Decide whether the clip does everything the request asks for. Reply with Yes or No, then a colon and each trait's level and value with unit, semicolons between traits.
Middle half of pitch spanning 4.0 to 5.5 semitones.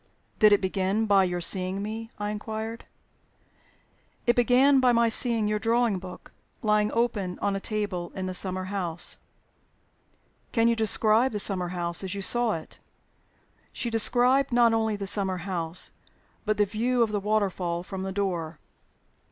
No: average, 3.3 semitones